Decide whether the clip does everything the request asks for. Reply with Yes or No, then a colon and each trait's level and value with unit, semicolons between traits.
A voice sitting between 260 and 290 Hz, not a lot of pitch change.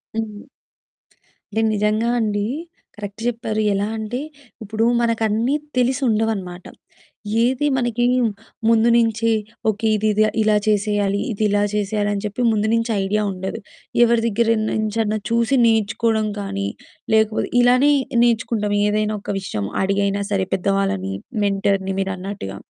No: high, 215 Hz; narrow, 2.1 semitones